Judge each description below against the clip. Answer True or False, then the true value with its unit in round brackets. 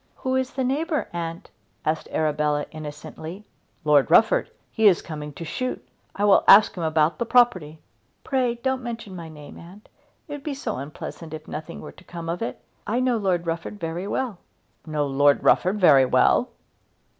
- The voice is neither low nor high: True (175 Hz)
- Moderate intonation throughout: False (7.2 semitones)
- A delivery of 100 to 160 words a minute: False (180 wpm)